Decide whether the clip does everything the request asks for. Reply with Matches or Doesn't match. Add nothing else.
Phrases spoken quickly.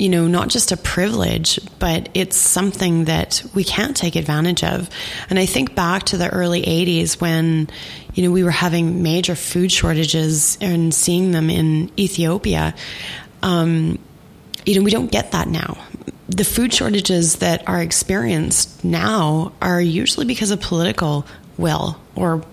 Doesn't match